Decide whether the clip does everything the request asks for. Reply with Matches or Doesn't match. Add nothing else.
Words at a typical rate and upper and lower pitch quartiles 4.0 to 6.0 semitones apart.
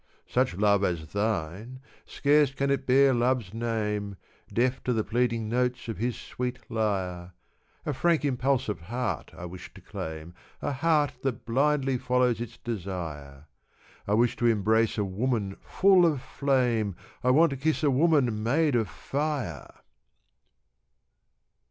Matches